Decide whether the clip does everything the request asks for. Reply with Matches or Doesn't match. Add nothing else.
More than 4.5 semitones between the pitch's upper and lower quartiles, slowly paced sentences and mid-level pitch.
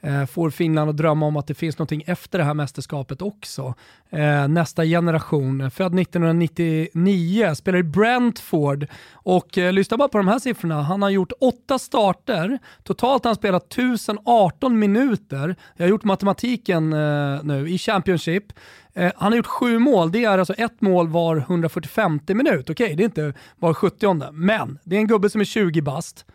Doesn't match